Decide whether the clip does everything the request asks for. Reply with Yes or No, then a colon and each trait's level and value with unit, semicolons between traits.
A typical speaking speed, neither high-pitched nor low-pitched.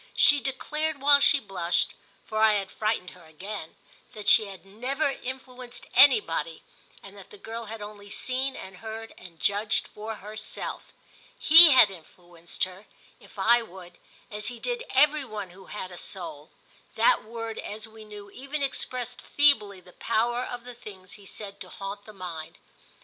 No: average, 165 wpm; high, 215 Hz